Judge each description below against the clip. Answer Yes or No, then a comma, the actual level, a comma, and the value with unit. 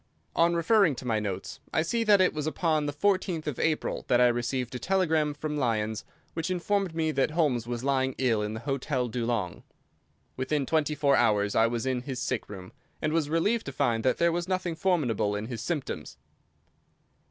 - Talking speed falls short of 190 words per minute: No, average, 200 wpm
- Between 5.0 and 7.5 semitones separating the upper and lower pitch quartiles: Yes, wide, 5.6 semitones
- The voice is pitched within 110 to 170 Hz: Yes, medium, 140 Hz